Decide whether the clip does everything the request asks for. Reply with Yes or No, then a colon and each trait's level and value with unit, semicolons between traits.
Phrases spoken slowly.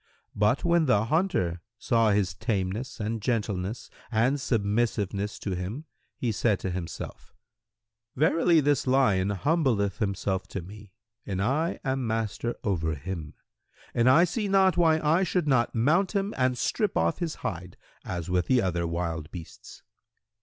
No: average, 155 wpm